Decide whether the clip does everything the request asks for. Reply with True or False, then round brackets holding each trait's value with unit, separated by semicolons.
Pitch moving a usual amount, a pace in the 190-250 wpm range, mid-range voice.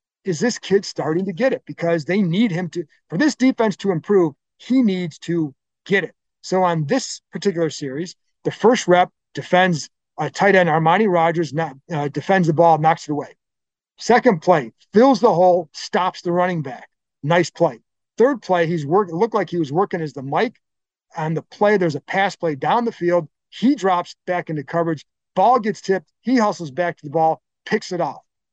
True (4.2 semitones; 200 wpm; 175 Hz)